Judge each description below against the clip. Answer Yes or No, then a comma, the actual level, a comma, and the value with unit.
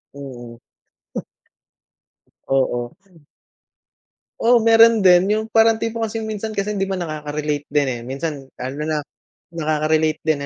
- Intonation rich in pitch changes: Yes, wide, 7.3 semitones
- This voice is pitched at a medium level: Yes, medium, 160 Hz